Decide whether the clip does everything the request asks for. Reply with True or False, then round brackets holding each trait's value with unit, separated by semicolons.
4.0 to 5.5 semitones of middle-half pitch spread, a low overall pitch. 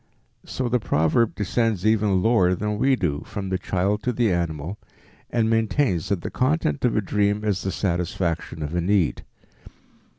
True (4.3 semitones; 100 Hz)